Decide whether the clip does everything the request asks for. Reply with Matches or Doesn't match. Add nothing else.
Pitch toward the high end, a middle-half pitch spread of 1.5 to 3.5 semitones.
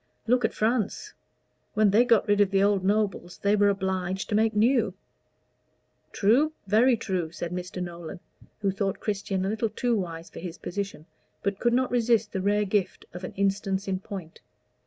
Matches